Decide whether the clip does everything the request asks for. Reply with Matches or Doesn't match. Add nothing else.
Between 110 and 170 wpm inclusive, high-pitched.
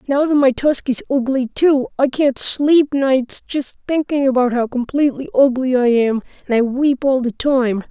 Doesn't match